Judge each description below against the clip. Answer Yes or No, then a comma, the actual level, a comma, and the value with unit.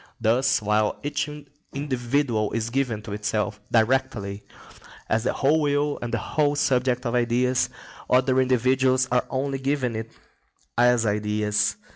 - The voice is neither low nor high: No, low, 125 Hz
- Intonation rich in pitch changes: No, average, 3.2 semitones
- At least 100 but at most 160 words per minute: Yes, slow, 135 wpm